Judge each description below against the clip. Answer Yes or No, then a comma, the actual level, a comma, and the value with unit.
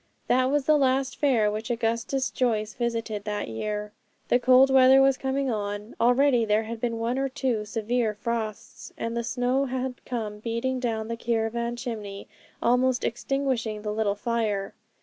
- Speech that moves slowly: No, average, 165 wpm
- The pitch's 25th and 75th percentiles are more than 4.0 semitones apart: No, average, 3.0 semitones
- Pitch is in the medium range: No, high, 235 Hz